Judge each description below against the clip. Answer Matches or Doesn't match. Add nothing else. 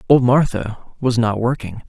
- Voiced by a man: Matches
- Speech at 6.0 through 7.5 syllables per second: Doesn't match